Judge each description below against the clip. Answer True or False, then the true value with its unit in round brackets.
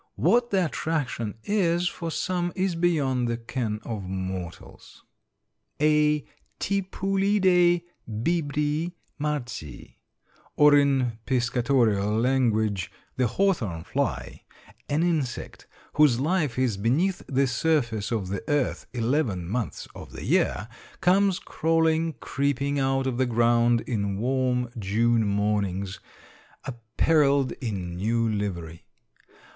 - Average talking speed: False (110 wpm)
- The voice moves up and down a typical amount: False (6.4 semitones)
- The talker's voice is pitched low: True (130 Hz)